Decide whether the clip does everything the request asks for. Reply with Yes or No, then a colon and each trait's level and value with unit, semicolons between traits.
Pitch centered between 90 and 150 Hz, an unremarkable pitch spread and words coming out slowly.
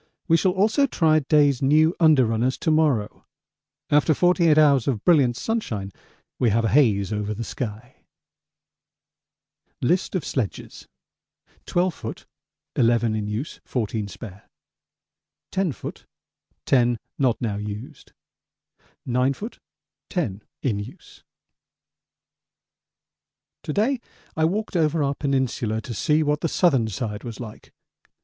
No: low, 135 Hz; wide, 6.1 semitones; slow, 125 wpm